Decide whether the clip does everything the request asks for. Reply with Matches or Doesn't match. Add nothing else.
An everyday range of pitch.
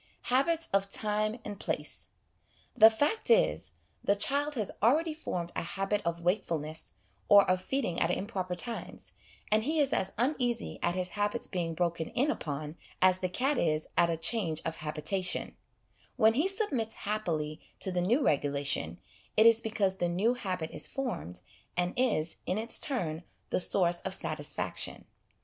Doesn't match